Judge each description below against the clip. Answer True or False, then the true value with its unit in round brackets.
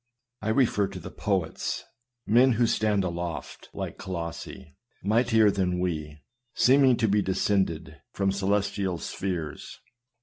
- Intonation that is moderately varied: True (3.8 semitones)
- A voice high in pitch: False (100 Hz)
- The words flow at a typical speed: False (125 wpm)